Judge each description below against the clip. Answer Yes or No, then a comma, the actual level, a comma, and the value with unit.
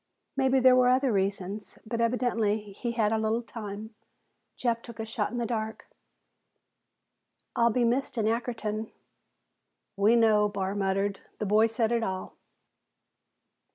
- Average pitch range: No, narrow, 2.3 semitones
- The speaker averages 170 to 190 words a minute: No, average, 145 wpm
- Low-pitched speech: No, high, 225 Hz